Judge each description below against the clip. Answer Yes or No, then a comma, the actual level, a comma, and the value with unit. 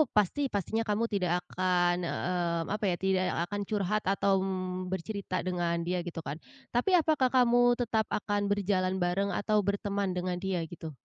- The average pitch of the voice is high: Yes, high, 195 Hz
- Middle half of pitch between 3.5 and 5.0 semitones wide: No, average, 2.8 semitones